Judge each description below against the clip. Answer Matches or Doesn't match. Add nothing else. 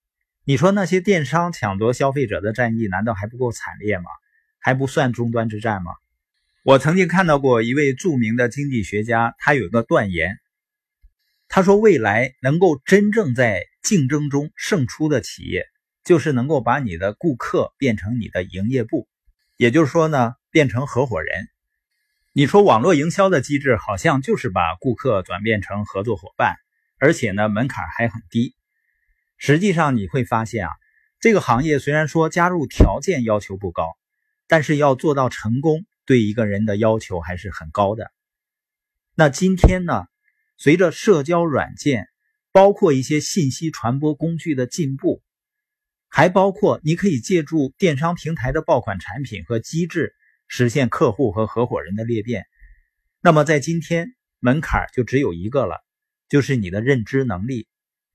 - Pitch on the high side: Doesn't match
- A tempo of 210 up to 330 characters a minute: Matches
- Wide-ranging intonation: Matches